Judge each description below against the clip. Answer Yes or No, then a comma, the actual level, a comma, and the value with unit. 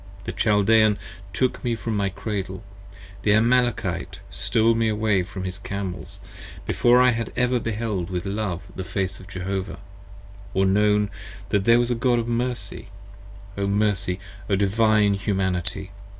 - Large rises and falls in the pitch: No, average, 3.0 semitones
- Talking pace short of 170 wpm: Yes, average, 150 wpm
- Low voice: Yes, low, 105 Hz